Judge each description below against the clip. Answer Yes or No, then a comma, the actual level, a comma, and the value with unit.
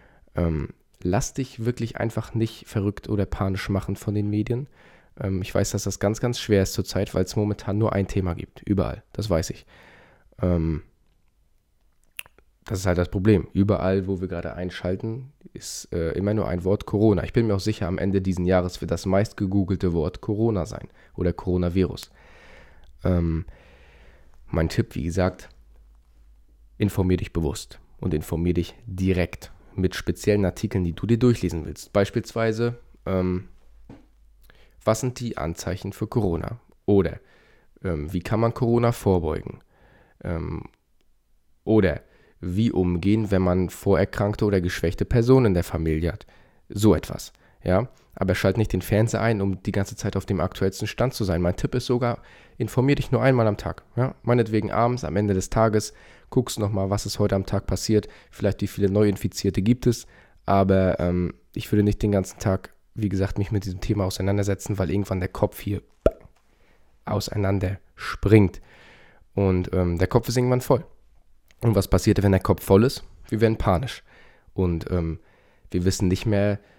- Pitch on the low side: Yes, low, 100 Hz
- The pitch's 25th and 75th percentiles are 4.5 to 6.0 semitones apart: No, average, 3.3 semitones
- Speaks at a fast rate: No, average, 170 wpm